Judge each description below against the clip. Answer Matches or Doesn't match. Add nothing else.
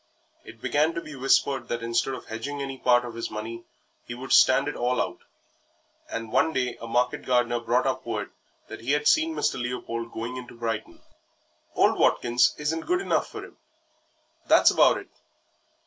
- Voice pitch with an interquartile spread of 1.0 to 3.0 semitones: Matches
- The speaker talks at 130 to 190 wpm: Matches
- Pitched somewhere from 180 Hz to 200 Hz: Doesn't match